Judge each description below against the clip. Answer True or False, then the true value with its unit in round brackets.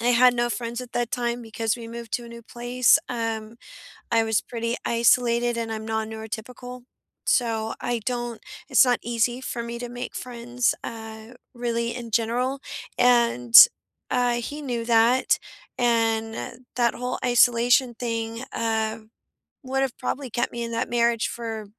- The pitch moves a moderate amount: False (1.2 semitones)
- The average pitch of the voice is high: True (235 Hz)